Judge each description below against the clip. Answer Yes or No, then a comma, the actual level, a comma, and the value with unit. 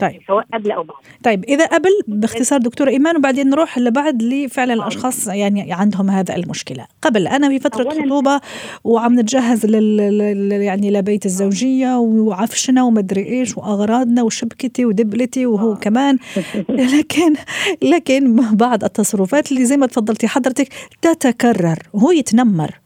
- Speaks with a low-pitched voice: No, high, 240 Hz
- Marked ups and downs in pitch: No, average, 4.3 semitones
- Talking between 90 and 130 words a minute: Yes, average, 120 wpm